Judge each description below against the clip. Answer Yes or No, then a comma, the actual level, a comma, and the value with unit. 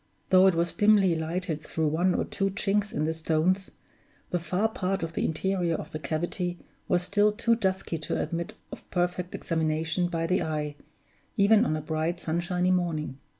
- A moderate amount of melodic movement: Yes, average, 3.0 semitones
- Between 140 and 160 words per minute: No, average, 180 wpm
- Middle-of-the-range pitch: Yes, medium, 175 Hz